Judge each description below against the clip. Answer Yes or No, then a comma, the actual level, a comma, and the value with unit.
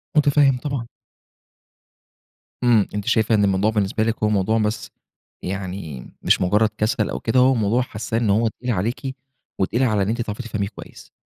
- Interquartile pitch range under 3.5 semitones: Yes, average, 3.1 semitones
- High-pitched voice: No, low, 110 Hz